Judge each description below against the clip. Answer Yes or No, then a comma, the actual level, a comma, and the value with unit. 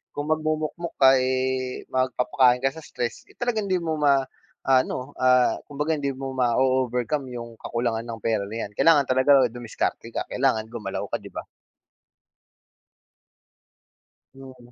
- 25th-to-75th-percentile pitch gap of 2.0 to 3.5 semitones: Yes, average, 2.8 semitones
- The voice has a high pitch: No, low, 130 Hz